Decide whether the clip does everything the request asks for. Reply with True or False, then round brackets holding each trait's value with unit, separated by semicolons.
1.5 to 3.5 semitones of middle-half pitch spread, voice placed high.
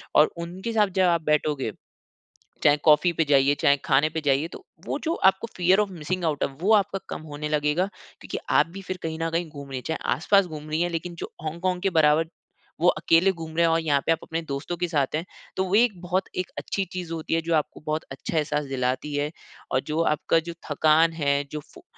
False (3.0 semitones; 160 Hz)